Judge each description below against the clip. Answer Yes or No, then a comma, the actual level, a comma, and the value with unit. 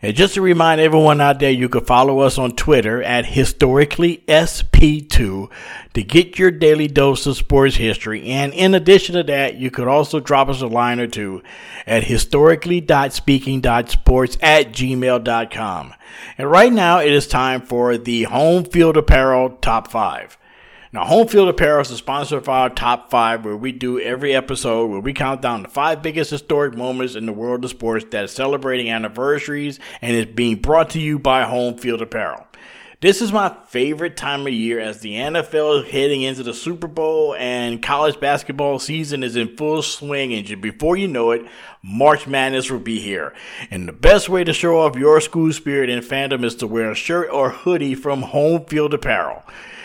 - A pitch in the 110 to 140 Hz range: Yes, low, 135 Hz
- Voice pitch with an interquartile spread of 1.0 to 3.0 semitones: No, average, 4.2 semitones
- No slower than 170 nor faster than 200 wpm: Yes, average, 185 wpm